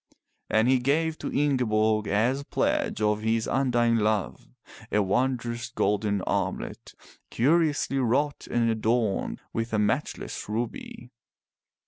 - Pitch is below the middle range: Yes, low, 115 Hz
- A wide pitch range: No, average, 3.7 semitones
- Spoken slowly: Yes, slow, 115 wpm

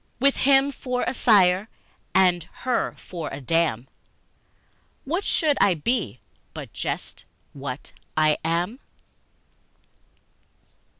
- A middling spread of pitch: No, wide, 8.4 semitones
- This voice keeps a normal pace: No, slow, 105 wpm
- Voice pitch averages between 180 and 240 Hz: Yes, medium, 185 Hz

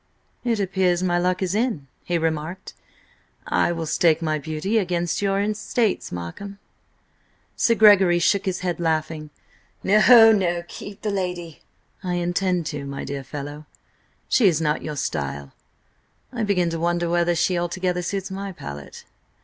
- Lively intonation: No, average, 3.4 semitones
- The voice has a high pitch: No, medium, 175 Hz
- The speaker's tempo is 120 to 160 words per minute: Yes, average, 150 wpm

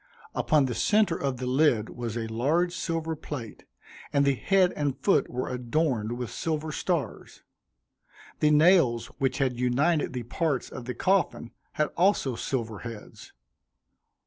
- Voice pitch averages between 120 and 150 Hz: Yes, low, 135 Hz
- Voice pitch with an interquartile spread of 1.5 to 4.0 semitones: No, average, 4.8 semitones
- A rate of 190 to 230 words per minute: No, average, 145 wpm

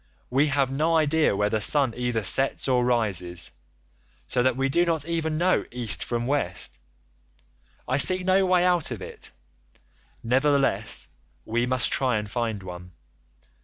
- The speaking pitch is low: Yes, low, 130 Hz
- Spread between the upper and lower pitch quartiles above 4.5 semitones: Yes, average, 5.3 semitones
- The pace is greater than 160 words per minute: No, average, 155 wpm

